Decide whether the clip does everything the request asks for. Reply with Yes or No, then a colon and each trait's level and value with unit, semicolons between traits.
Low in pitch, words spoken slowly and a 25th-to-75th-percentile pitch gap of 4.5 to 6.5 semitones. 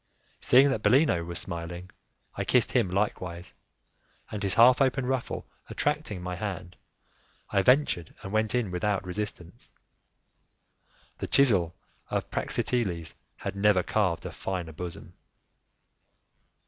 Yes: low, 100 Hz; slow, 120 wpm; wide, 5.4 semitones